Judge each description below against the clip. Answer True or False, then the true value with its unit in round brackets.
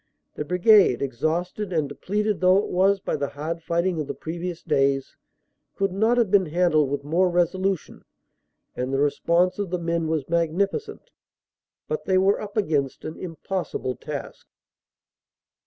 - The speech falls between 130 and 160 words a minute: True (155 wpm)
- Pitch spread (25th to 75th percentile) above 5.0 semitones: False (3.9 semitones)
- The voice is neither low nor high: True (175 Hz)